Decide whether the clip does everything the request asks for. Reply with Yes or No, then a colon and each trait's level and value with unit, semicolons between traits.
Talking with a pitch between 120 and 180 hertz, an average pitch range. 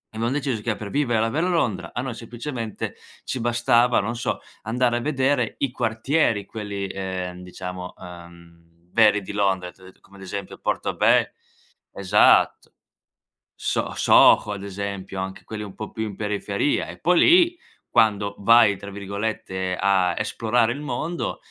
No: low, 105 Hz; average, 3.8 semitones